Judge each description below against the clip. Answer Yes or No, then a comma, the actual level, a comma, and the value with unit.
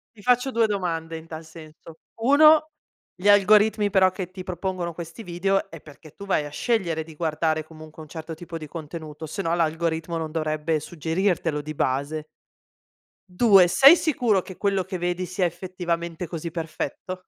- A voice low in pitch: No, medium, 170 Hz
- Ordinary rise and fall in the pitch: Yes, average, 3.3 semitones